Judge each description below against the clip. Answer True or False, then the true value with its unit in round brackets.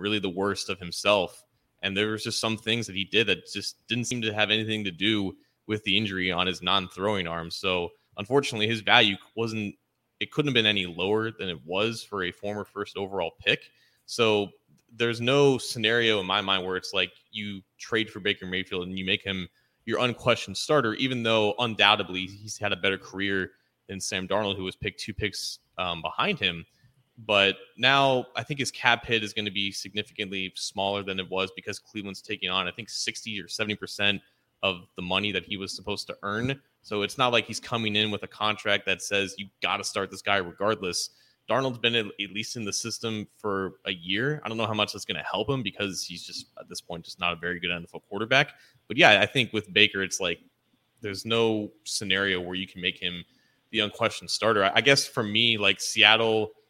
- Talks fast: True (215 wpm)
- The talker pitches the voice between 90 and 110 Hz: True (105 Hz)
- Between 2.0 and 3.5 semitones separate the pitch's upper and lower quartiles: True (2.8 semitones)